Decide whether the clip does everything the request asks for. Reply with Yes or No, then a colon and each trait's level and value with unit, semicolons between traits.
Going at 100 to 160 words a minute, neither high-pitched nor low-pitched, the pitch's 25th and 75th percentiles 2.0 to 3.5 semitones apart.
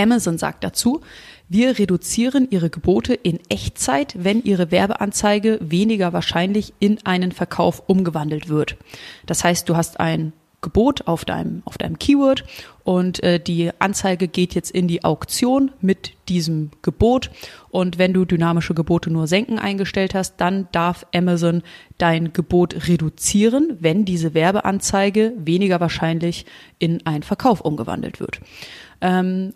Yes: average, 140 wpm; medium, 180 Hz; average, 3.2 semitones